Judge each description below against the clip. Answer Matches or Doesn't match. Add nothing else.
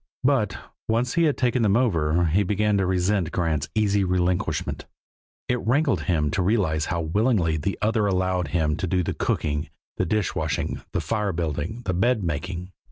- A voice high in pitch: Doesn't match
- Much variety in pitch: Doesn't match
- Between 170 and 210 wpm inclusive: Matches